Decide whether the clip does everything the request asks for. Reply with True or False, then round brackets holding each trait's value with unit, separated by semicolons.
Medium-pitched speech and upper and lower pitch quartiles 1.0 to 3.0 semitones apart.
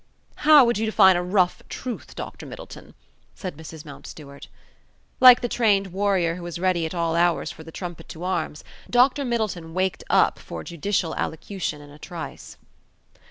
False (180 Hz; 4.1 semitones)